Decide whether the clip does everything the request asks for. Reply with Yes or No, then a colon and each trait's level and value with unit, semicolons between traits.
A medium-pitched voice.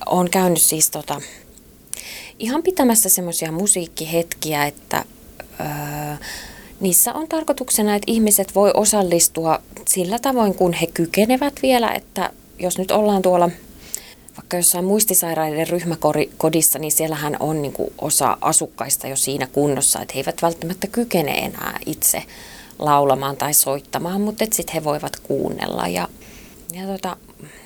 Yes: medium, 175 Hz